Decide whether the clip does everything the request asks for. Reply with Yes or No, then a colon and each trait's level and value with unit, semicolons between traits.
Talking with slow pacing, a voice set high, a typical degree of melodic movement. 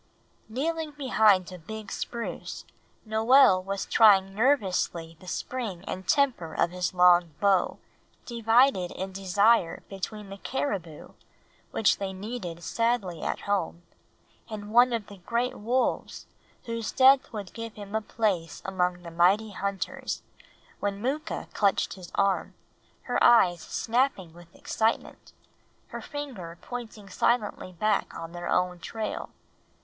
Yes: slow, 130 wpm; high, 200 Hz; average, 4.3 semitones